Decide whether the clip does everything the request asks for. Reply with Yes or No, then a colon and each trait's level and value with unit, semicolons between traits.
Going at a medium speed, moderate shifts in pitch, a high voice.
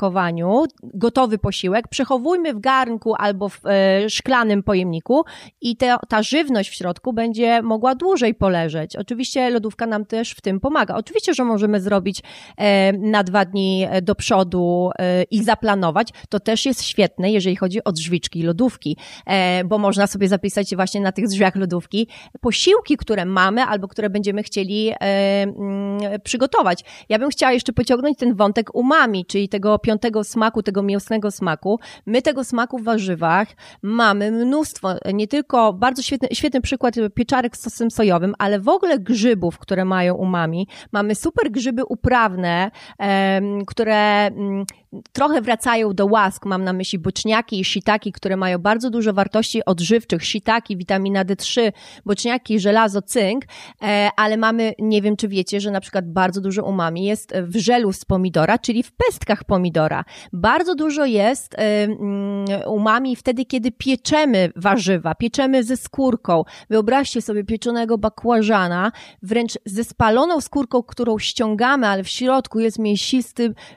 Yes: average, 145 wpm; average, 3.5 semitones; high, 215 Hz